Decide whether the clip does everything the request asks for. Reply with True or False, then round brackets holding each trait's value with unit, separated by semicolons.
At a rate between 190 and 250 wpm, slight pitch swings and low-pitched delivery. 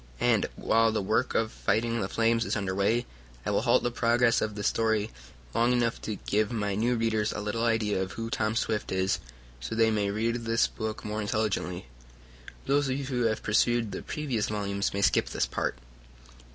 True (200 wpm; 2.0 semitones; 110 Hz)